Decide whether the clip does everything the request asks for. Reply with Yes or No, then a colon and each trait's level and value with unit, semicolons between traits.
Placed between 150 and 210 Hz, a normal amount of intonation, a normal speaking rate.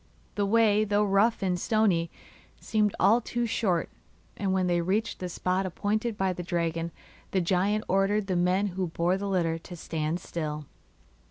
Yes: high, 190 Hz; average, 3.0 semitones; average, 170 wpm